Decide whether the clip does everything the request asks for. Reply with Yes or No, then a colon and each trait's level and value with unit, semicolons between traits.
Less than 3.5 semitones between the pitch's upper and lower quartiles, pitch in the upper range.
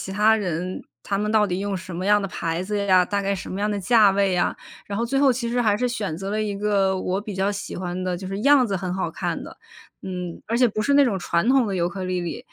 Yes: narrow, 2.5 semitones; high, 200 Hz